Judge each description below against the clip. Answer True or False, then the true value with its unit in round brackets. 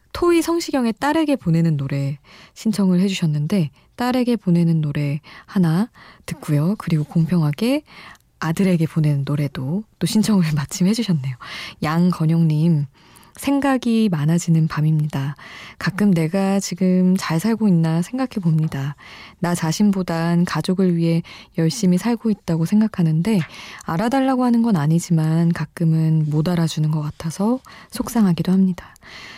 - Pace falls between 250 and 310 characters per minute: True (305 characters per minute)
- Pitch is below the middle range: False (175 Hz)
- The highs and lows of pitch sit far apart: False (4.7 semitones)